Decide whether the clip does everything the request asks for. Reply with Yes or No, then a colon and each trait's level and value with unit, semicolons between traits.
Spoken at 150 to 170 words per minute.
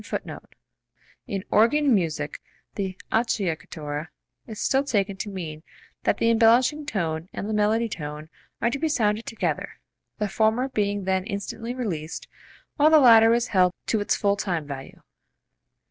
Yes: average, 155 wpm